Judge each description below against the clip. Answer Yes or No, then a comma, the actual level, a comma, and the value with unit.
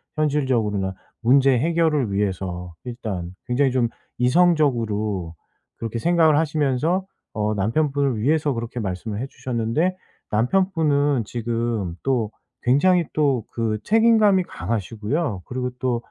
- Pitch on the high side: No, low, 125 Hz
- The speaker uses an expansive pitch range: Yes, wide, 5.8 semitones